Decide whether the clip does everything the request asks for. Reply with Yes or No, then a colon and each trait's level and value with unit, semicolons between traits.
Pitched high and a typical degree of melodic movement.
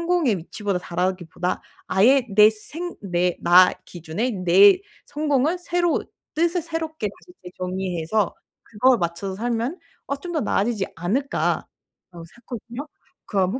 No: high, 215 Hz; wide, 7.6 semitones